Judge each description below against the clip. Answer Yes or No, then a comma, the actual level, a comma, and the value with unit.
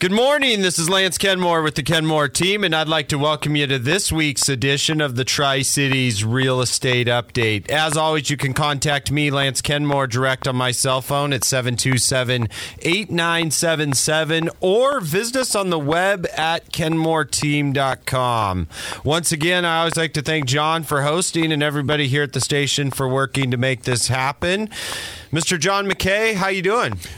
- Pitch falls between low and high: Yes, medium, 150 Hz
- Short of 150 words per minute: No, average, 170 wpm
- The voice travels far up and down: No, average, 3.9 semitones